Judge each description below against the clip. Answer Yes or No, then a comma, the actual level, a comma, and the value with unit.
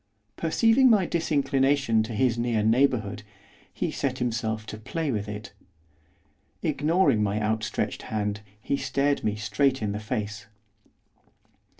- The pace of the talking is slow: Yes, slow, 125 wpm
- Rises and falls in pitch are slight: No, average, 4.8 semitones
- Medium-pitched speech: No, low, 115 Hz